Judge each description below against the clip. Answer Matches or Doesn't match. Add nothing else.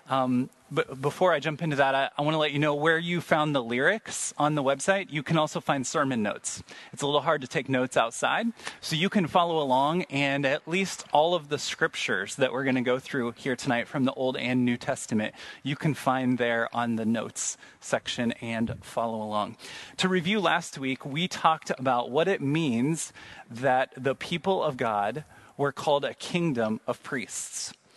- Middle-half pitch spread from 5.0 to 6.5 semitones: Doesn't match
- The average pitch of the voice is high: Doesn't match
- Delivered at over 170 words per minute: Matches